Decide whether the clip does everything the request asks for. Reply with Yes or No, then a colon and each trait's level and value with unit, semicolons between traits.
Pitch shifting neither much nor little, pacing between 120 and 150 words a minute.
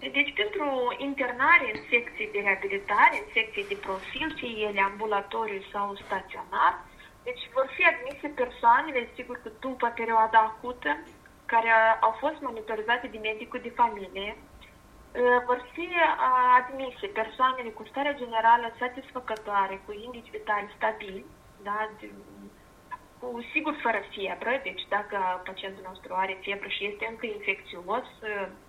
Yes: average, 4.0 semitones; average, 130 wpm